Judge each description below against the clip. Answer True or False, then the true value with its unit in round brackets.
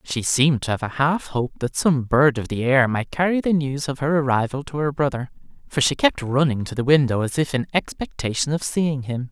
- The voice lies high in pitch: False (140 Hz)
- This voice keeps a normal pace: False (240 wpm)